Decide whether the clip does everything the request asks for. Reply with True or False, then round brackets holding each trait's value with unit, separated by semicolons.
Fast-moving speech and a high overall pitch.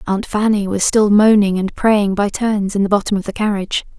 True (225 wpm; 205 Hz)